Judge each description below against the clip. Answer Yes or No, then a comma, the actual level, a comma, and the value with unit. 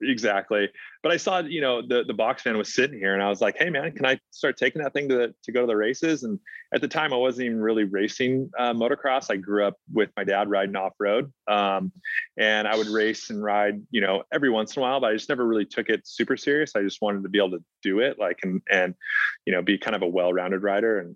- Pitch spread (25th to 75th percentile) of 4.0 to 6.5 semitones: Yes, average, 4.3 semitones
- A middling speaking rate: No, fast, 270 wpm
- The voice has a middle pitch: No, low, 105 Hz